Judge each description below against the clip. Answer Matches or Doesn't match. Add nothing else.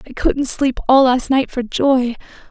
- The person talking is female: Matches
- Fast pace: Doesn't match